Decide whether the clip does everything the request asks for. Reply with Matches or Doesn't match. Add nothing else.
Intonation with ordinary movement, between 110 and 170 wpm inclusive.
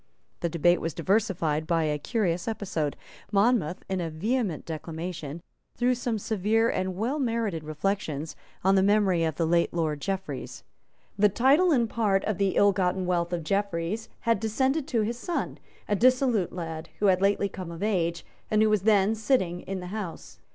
Doesn't match